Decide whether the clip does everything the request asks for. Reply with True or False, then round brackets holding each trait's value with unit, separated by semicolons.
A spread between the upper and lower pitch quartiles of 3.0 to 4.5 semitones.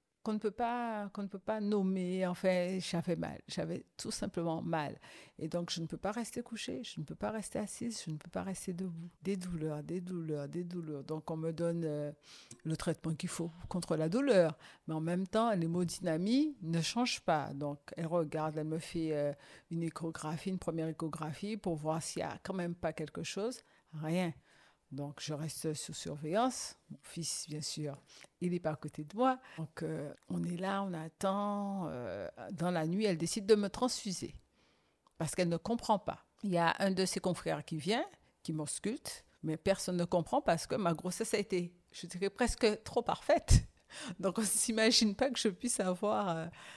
True (4.1 semitones)